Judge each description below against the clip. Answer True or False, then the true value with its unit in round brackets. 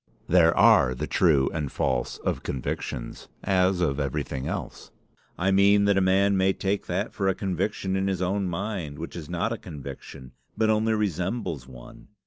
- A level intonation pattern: False (4.6 semitones)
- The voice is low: True (95 Hz)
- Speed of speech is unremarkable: True (175 wpm)